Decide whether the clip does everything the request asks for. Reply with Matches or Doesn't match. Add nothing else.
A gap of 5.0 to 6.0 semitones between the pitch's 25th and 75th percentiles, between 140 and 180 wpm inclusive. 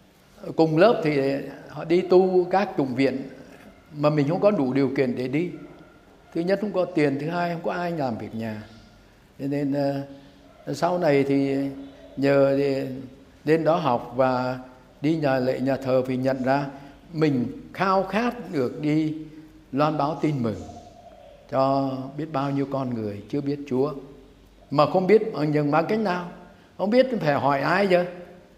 Doesn't match